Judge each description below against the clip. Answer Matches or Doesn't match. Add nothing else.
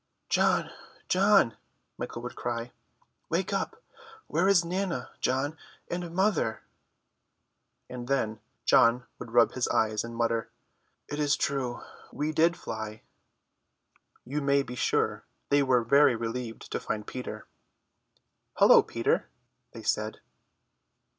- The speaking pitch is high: Doesn't match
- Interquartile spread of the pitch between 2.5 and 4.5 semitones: Doesn't match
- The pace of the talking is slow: Matches